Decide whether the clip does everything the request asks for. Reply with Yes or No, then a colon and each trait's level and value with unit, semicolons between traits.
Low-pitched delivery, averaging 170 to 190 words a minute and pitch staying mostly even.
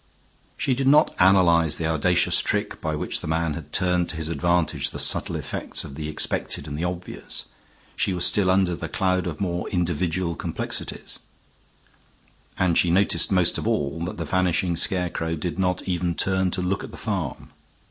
Yes: very low, 90 Hz; average, 180 wpm; narrow, 2.2 semitones